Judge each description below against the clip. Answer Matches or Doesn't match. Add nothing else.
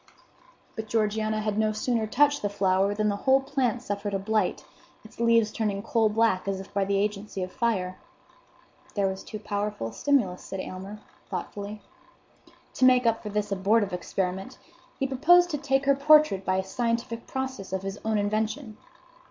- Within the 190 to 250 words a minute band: Doesn't match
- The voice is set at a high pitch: Matches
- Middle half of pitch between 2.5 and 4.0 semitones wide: Matches